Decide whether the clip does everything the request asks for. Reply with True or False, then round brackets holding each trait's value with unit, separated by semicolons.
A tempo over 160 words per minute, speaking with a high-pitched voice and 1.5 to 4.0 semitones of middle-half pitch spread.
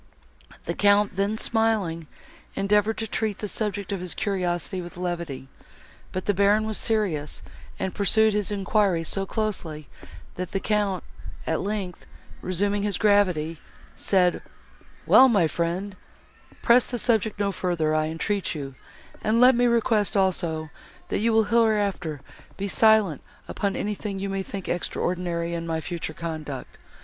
False (145 wpm; 195 Hz; 3.5 semitones)